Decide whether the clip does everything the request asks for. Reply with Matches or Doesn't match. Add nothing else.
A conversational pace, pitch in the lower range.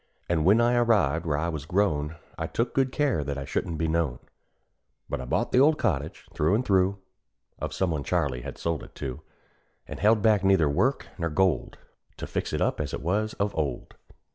Doesn't match